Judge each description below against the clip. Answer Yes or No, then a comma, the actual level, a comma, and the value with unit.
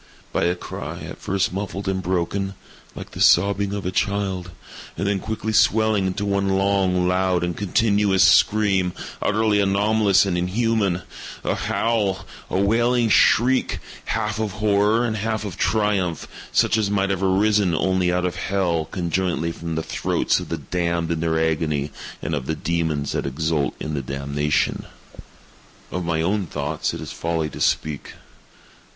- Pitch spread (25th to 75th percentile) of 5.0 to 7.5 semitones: No, average, 3.4 semitones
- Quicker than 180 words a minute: No, average, 160 wpm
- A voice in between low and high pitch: No, very low, 95 Hz